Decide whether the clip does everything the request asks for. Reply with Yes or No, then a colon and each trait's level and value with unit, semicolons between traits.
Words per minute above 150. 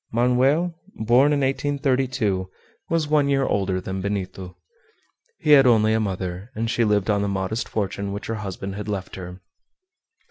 Yes: average, 165 wpm